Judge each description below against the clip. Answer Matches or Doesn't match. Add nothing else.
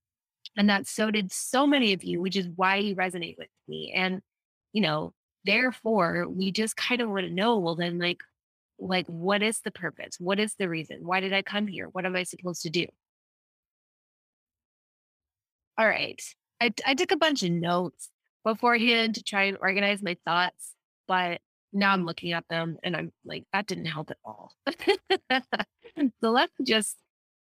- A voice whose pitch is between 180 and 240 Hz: Matches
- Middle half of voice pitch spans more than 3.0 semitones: Matches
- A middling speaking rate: Matches